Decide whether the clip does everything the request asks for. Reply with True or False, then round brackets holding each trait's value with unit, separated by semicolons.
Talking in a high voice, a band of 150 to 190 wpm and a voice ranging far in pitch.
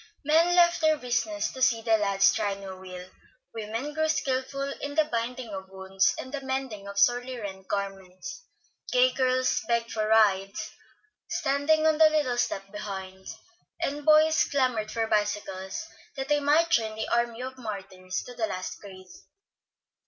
True (235 Hz; 160 wpm; 6.1 semitones)